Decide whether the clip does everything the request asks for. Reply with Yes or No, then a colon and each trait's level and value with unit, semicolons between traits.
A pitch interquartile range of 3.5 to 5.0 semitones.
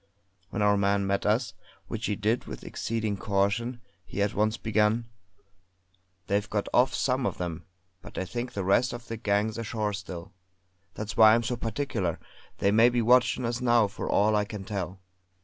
No: average, 2.7 semitones